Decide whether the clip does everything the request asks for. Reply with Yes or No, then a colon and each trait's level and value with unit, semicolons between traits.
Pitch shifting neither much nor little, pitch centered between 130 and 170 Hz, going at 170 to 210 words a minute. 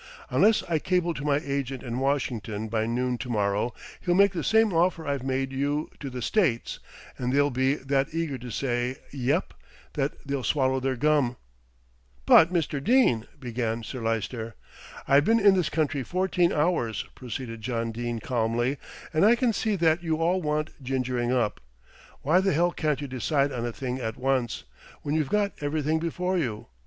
Yes: average, 4.9 semitones; low, 135 Hz; average, 180 wpm